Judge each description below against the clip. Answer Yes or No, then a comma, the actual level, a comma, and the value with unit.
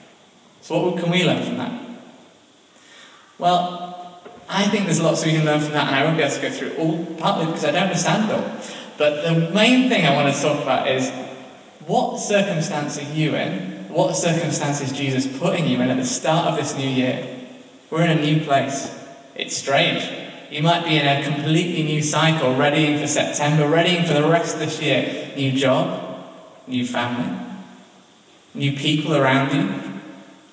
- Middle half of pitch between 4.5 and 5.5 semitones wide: No, average, 3.5 semitones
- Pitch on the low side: No, medium, 155 Hz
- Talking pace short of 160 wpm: No, average, 185 wpm